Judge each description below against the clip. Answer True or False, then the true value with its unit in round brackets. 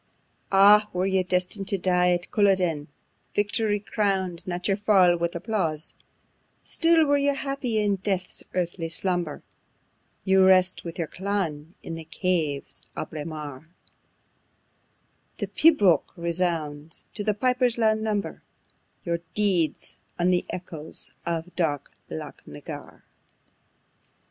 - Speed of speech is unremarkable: False (125 wpm)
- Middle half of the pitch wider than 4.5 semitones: False (3.6 semitones)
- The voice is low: False (185 Hz)